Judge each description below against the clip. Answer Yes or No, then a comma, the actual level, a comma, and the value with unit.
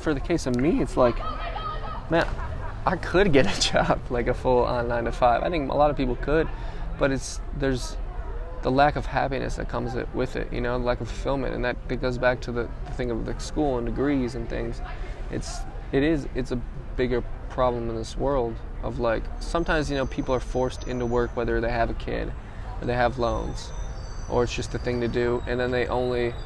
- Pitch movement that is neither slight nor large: No, narrow, 1.7 semitones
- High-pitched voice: No, low, 125 Hz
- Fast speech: Yes, fast, 220 wpm